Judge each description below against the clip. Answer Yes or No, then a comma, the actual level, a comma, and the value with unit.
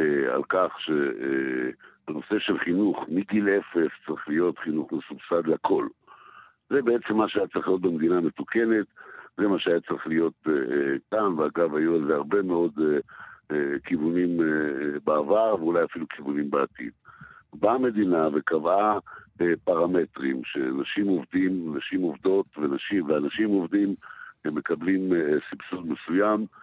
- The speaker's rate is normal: No, slow, 120 wpm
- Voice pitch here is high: No, very low, 90 Hz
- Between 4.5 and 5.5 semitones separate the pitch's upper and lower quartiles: Yes, average, 4.8 semitones